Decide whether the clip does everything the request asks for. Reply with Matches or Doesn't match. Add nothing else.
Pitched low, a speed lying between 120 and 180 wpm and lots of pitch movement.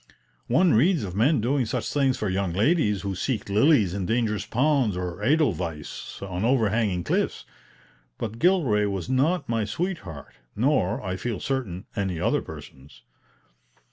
Matches